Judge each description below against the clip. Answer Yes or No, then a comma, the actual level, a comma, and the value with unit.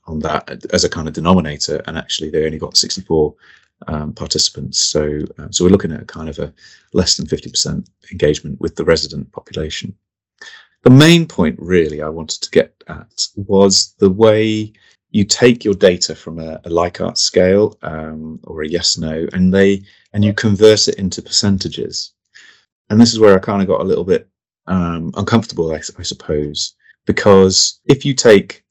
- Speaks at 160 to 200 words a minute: Yes, average, 180 wpm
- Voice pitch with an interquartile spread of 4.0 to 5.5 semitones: Yes, average, 4.9 semitones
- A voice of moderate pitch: No, very low, 95 Hz